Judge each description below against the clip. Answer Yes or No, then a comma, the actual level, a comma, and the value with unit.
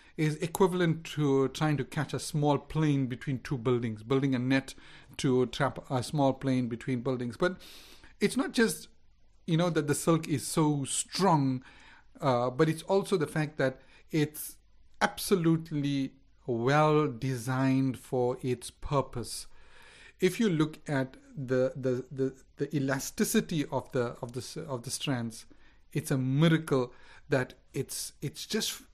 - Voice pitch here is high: No, low, 135 Hz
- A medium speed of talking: Yes, average, 145 wpm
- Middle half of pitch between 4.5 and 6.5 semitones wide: No, average, 3.4 semitones